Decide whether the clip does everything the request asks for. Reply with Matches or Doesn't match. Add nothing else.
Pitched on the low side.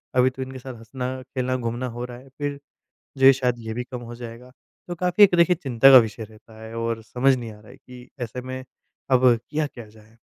Matches